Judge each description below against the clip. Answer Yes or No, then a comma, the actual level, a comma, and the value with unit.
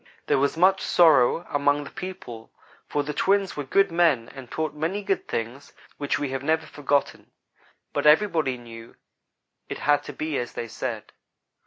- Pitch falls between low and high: Yes, medium, 145 Hz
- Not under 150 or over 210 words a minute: Yes, average, 170 wpm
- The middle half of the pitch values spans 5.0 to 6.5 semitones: No, average, 4.2 semitones